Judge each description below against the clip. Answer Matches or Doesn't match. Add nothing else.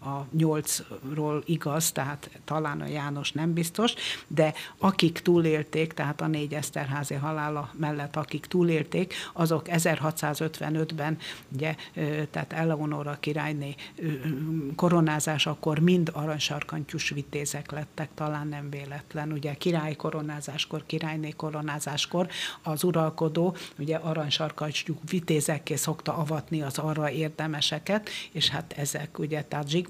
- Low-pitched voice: Doesn't match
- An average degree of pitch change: Doesn't match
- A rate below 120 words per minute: Matches